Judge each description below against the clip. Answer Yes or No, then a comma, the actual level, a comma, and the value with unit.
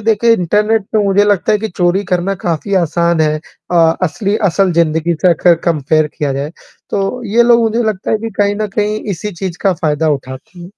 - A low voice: No, high, 190 Hz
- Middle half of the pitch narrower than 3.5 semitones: No, average, 4.2 semitones